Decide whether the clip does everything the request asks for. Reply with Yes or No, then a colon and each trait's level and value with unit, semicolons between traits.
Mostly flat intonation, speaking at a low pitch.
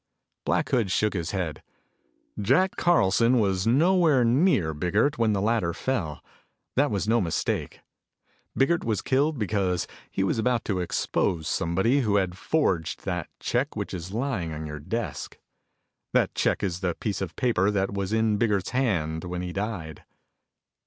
No: average, 5.2 semitones; low, 100 Hz